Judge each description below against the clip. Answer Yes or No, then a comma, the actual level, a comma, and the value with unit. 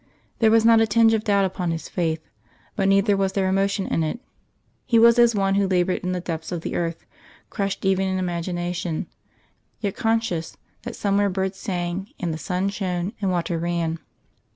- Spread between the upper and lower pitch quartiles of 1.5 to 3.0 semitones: Yes, narrow, 2.6 semitones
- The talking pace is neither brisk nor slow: Yes, average, 190 wpm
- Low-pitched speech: No, high, 190 Hz